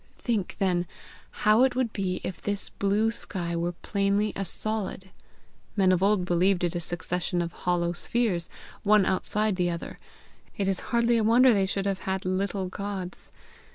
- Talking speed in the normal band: Yes, average, 170 wpm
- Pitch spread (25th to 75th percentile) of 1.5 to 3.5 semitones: Yes, average, 2.9 semitones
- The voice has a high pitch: Yes, high, 195 Hz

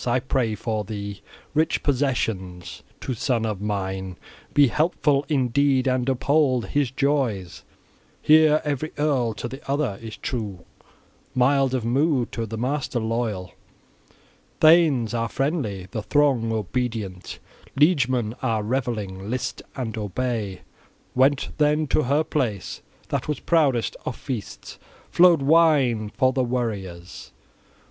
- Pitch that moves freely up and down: No, average, 4.7 semitones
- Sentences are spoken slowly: Yes, slow, 130 wpm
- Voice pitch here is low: Yes, low, 125 Hz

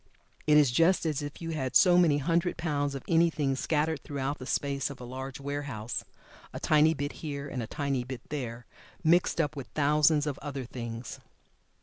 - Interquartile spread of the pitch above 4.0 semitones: No, average, 2.7 semitones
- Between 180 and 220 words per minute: Yes, average, 190 wpm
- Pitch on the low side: No, medium, 145 Hz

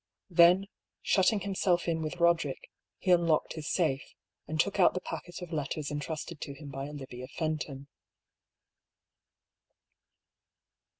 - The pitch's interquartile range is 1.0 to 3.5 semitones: Yes, average, 3.2 semitones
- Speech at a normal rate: No, slow, 125 wpm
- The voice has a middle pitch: Yes, medium, 160 Hz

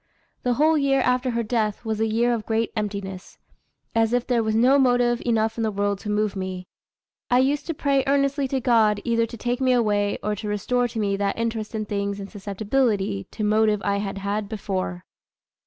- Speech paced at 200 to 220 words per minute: Yes, fast, 205 wpm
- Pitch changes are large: No, average, 3.2 semitones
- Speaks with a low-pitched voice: No, high, 220 Hz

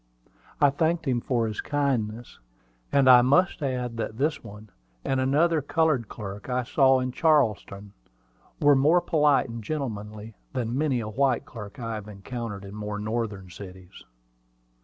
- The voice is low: Yes, low, 120 Hz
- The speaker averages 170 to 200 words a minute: No, average, 155 wpm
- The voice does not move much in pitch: No, average, 4.7 semitones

